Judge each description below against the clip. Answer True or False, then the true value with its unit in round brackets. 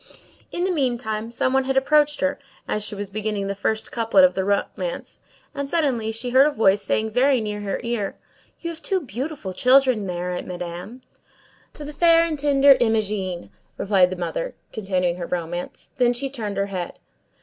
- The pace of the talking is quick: False (185 wpm)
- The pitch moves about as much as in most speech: False (5.8 semitones)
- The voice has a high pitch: True (225 Hz)